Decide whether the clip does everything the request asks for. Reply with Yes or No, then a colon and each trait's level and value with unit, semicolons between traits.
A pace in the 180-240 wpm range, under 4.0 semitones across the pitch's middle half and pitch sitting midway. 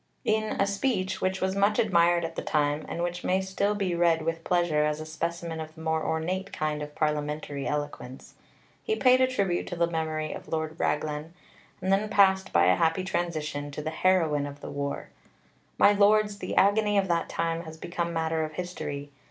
Yes: average, 200 wpm; average, 3.6 semitones; medium, 170 Hz